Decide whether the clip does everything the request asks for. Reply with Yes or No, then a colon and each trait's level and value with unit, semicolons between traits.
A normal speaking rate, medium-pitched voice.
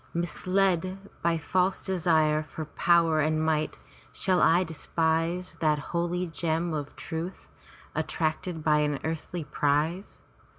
No: slow, 120 wpm; medium, 165 Hz